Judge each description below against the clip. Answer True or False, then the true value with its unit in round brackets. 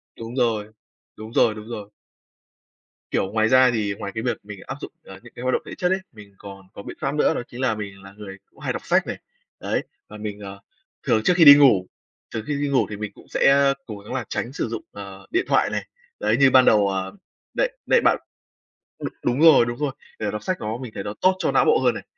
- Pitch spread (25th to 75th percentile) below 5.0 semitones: True (4.6 semitones)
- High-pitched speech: False (110 Hz)